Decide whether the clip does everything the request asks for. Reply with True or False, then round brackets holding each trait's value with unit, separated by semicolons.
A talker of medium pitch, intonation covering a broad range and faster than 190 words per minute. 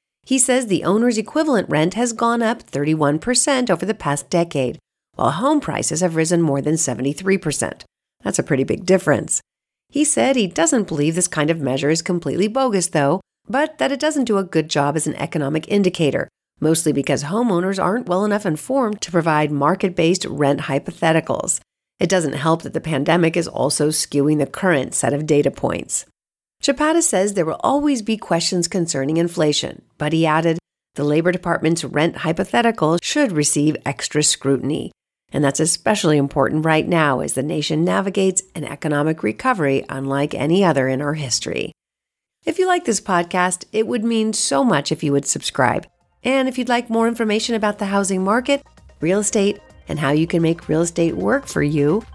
False (170 Hz; 5.7 semitones; 180 wpm)